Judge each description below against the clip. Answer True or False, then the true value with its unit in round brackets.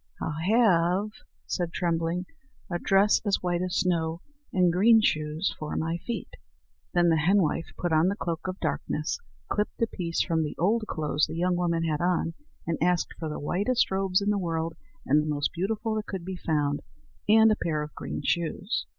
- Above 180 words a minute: True (190 wpm)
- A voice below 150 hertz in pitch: False (175 Hz)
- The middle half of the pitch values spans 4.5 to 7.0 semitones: False (3.1 semitones)